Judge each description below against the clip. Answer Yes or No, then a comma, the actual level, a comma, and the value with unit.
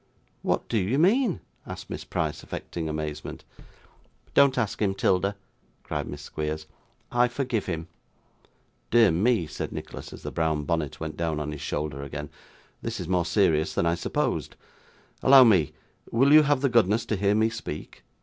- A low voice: Yes, very low, 95 Hz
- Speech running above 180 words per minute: No, average, 170 wpm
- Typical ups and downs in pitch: No, wide, 7.3 semitones